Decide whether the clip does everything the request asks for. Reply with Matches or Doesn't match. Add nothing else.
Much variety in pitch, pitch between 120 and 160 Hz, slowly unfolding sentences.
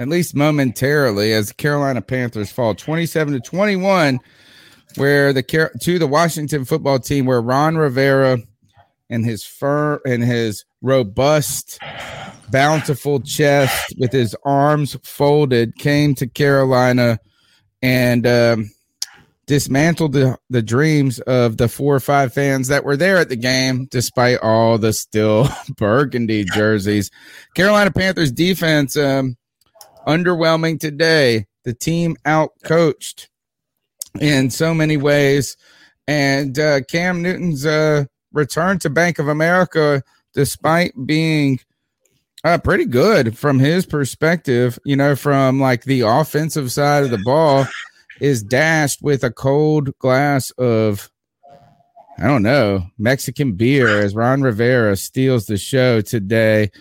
Doesn't match